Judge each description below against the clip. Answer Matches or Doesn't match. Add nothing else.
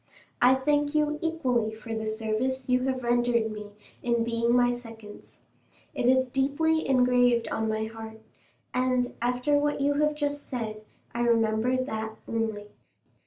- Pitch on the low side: Doesn't match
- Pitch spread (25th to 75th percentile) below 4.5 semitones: Matches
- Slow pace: Doesn't match